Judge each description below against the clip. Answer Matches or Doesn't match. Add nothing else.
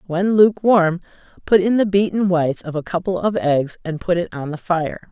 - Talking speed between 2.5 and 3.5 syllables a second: Doesn't match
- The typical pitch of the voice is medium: Matches